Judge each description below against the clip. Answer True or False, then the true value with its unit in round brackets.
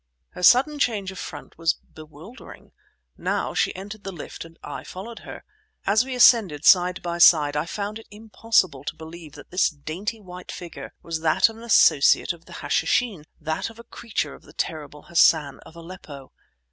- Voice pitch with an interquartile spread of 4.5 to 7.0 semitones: True (5.3 semitones)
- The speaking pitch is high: False (180 Hz)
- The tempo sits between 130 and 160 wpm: False (185 wpm)